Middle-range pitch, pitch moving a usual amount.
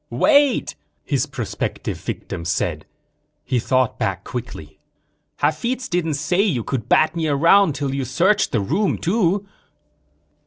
No: medium, 155 Hz; wide, 7.3 semitones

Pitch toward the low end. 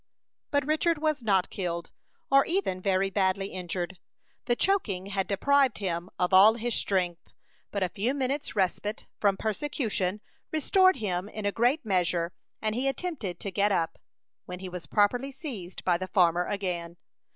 No: high, 200 Hz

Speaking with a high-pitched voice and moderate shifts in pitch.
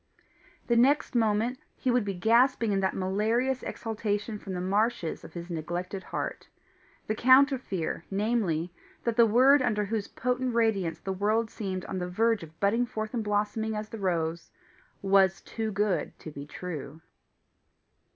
Yes: high, 210 Hz; average, 3.8 semitones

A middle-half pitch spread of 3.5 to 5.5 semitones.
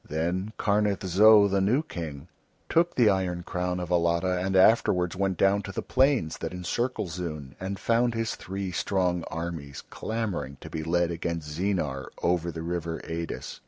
No: average, 3.1 semitones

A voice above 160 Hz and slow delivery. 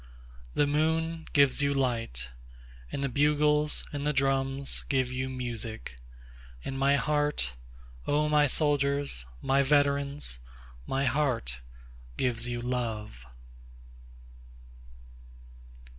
No: low, 135 Hz; slow, 90 wpm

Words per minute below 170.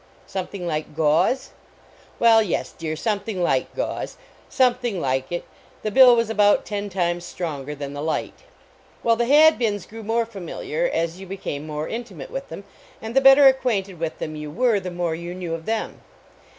No: average, 180 wpm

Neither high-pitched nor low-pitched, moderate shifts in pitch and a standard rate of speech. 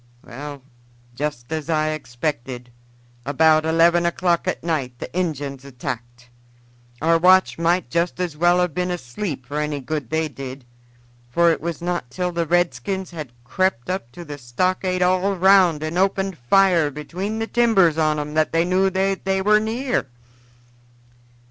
Yes: medium, 165 Hz; average, 4.2 semitones; average, 160 wpm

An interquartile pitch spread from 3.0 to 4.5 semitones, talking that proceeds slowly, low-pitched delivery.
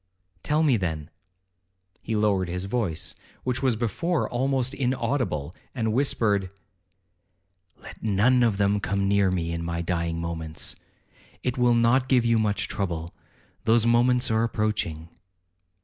No: average, 5.3 semitones; slow, 130 wpm; low, 110 Hz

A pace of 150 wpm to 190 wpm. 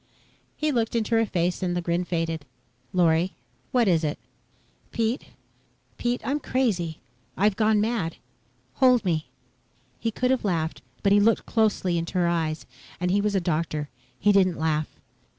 Yes: average, 165 wpm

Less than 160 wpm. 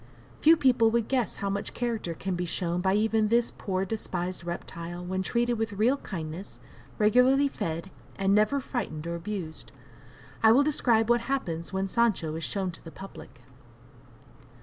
No: average, 165 wpm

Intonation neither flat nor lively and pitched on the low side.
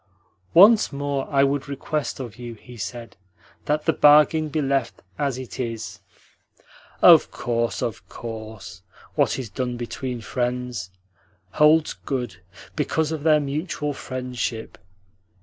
Yes: average, 3.9 semitones; low, 130 Hz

